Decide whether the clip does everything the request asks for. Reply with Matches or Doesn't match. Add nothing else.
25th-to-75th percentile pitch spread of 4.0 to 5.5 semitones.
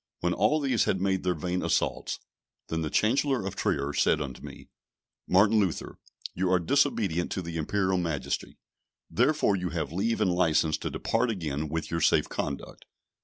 Matches